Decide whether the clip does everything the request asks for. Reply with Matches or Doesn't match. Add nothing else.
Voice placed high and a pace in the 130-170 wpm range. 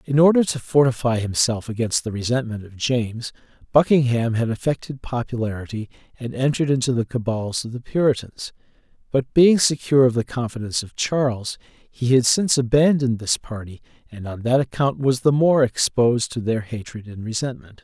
Doesn't match